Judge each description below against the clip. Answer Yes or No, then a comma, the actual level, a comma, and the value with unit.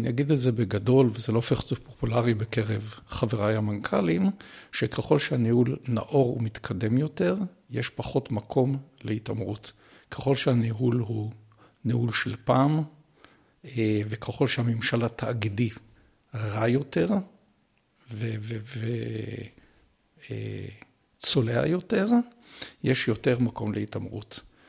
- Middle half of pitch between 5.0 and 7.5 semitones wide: No, average, 3.5 semitones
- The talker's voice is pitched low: Yes, low, 120 Hz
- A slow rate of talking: Yes, slow, 95 wpm